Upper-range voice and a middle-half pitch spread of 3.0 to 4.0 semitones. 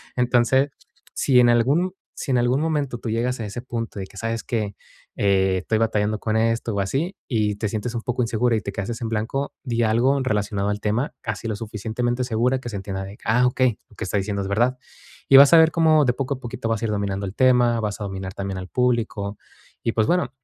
No: low, 115 Hz; average, 3.3 semitones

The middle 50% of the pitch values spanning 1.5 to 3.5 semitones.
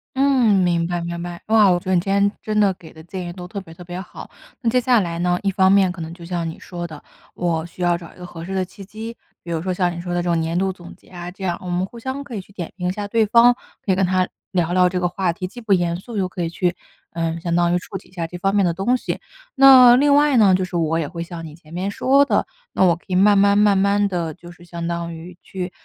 Yes: average, 2.7 semitones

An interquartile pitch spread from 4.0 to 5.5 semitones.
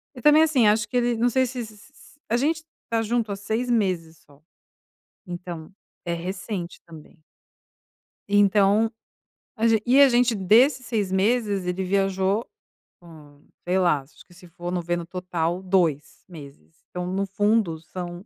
Yes: average, 4.6 semitones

